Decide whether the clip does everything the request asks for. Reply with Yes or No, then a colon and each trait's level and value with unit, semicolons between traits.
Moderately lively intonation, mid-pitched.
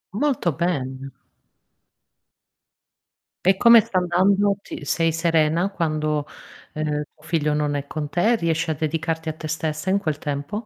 Yes: average, 3.1 semitones; medium, 160 Hz